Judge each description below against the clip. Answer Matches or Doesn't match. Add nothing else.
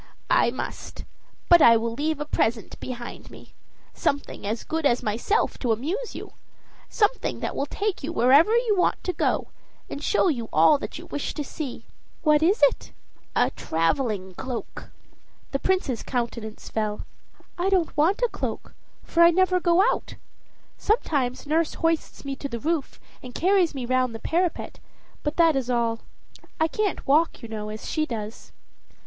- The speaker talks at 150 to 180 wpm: Matches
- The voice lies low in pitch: Doesn't match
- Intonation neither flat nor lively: Doesn't match